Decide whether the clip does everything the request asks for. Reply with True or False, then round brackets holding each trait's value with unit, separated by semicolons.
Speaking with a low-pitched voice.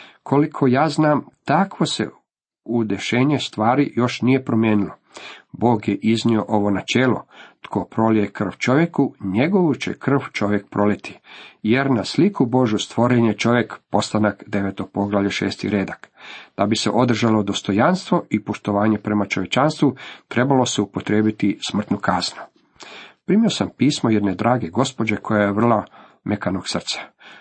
True (115 Hz)